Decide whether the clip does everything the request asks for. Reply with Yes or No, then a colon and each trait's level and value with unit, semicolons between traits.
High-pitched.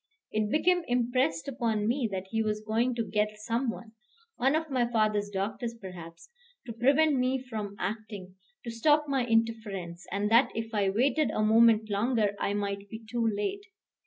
Yes: high, 225 Hz